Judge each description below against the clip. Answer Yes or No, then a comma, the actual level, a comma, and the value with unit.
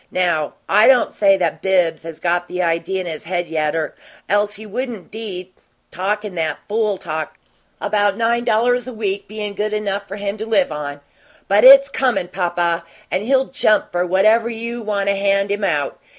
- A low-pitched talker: No, high, 200 Hz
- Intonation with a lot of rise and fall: No, average, 3.5 semitones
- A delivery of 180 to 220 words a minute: Yes, average, 190 wpm